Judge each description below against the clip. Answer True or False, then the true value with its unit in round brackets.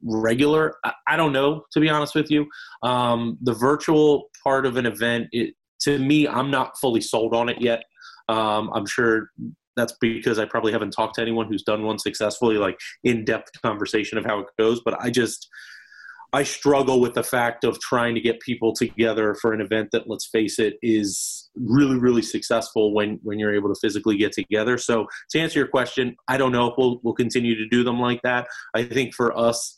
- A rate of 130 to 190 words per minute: False (205 wpm)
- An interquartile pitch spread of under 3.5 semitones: True (2.6 semitones)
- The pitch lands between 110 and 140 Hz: True (120 Hz)